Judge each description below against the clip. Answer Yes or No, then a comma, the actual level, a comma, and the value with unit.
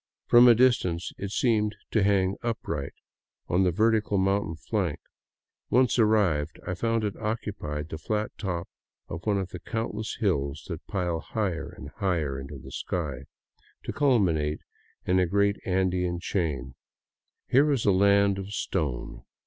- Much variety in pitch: No, average, 4.7 semitones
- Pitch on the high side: No, very low, 95 Hz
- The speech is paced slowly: No, average, 150 wpm